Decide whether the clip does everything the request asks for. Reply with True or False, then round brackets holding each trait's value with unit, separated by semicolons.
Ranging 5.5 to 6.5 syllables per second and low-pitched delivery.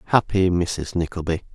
False (5.0 syllables/s; 90 Hz)